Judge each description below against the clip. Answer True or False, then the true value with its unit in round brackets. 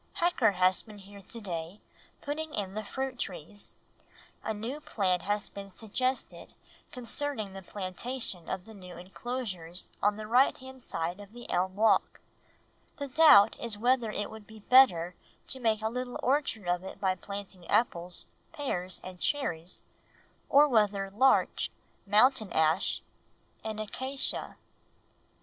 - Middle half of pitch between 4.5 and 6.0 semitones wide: True (5.1 semitones)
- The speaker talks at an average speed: True (145 wpm)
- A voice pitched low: False (210 Hz)